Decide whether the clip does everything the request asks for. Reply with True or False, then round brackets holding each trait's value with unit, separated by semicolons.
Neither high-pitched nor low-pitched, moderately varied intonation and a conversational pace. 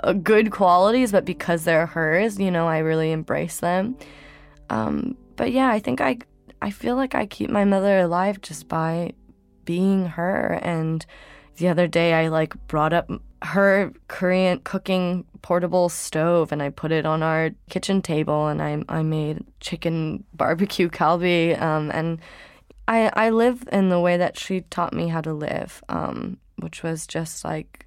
True (175 Hz; 3.2 semitones; 170 wpm)